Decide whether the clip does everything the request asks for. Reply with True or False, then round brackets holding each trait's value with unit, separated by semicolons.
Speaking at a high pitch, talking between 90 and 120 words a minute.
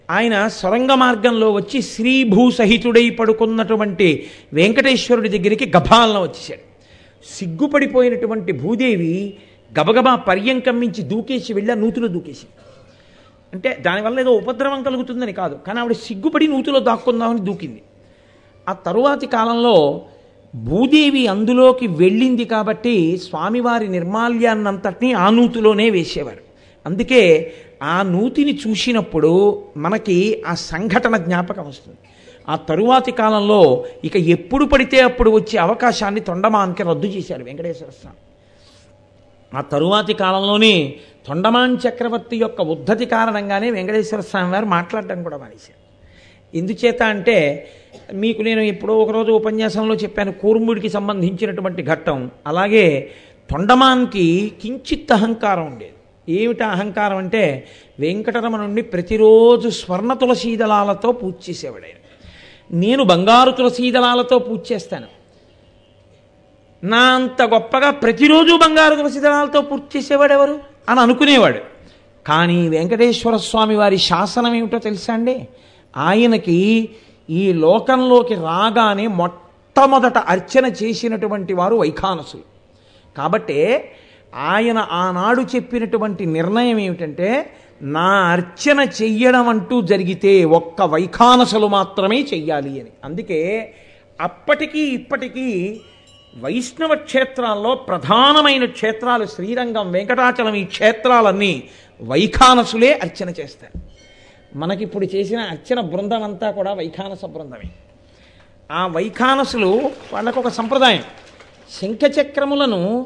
True (220 Hz; 100 wpm)